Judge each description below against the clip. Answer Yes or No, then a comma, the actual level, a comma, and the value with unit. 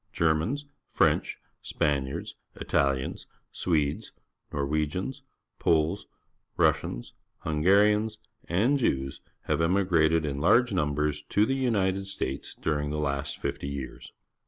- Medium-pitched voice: No, very low, 80 Hz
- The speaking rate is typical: No, slow, 120 wpm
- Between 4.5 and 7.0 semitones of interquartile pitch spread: Yes, wide, 5.5 semitones